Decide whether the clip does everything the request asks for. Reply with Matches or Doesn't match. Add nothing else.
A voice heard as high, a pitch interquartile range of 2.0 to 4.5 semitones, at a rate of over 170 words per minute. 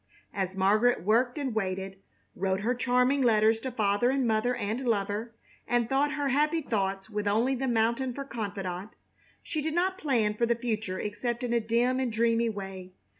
Matches